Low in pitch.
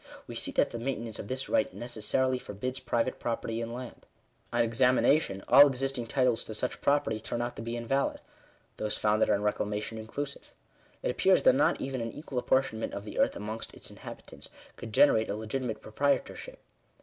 Yes: low, 120 Hz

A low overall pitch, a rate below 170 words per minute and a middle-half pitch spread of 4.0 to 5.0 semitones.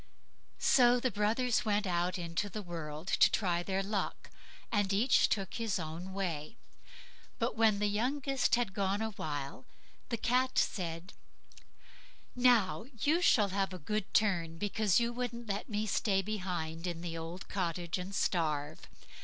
No: high, 195 Hz; average, 155 wpm; average, 4.3 semitones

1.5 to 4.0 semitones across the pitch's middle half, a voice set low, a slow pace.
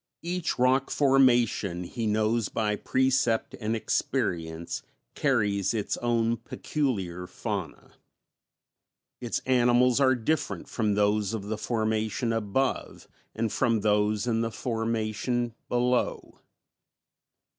Yes: average, 2.8 semitones; low, 115 Hz; slow, 105 wpm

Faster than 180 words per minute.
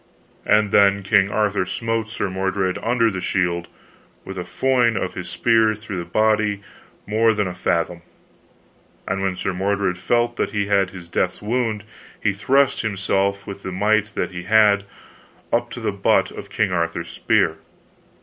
No: average, 170 wpm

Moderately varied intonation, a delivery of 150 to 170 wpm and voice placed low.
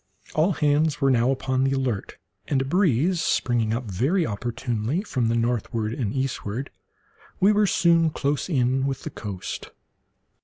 Yes: average, 4.7 semitones; average, 155 wpm; low, 130 Hz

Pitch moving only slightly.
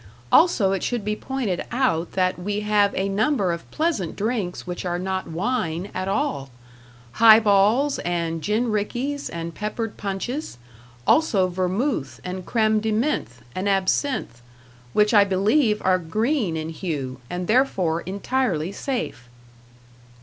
No: average, 4.5 semitones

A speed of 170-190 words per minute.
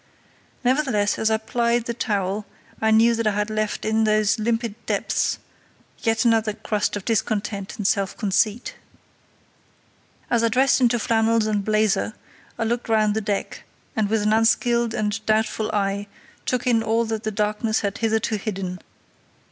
No: average, 160 wpm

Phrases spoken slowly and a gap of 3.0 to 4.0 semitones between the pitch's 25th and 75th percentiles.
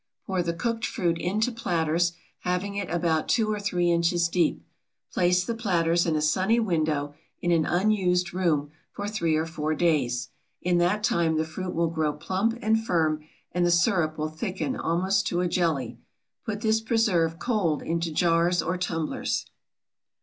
No: average, 170 wpm; average, 3.3 semitones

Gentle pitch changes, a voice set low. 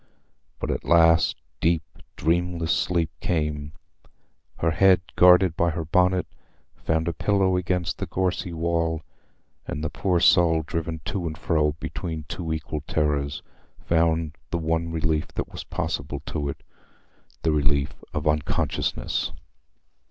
Yes: narrow, 2.0 semitones; very low, 80 Hz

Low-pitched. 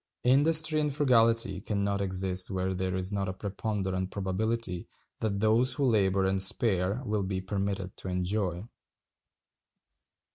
Yes: low, 100 Hz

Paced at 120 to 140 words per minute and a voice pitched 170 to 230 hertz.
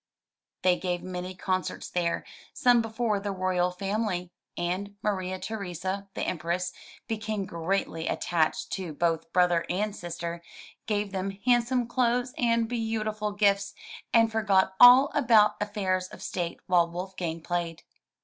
Yes: slow, 135 wpm; high, 190 Hz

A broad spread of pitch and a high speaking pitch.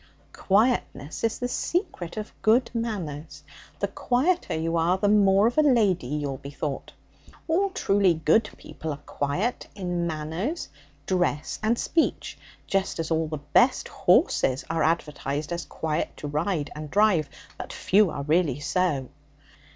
No: wide, 6.1 semitones; medium, 175 Hz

